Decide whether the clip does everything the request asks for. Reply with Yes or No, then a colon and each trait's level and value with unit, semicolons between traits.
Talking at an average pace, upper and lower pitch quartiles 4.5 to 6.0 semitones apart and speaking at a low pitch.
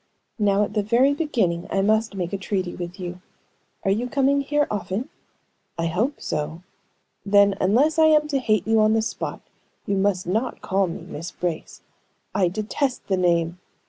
No: average, 175 wpm; average, 5.1 semitones; high, 205 Hz